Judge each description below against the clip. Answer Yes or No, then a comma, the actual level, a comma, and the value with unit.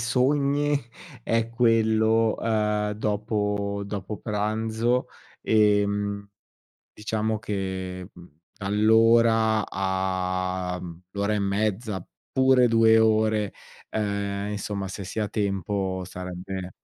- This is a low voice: Yes, low, 105 Hz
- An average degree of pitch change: No, narrow, 2.3 semitones